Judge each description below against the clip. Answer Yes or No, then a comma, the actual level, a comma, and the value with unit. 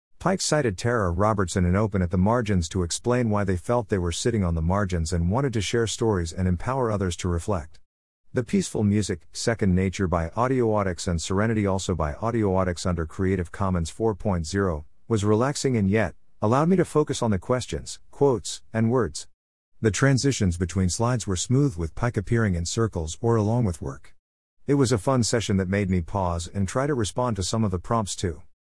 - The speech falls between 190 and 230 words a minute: Yes, average, 195 wpm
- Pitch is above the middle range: No, low, 100 Hz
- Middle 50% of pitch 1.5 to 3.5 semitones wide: No, average, 4.7 semitones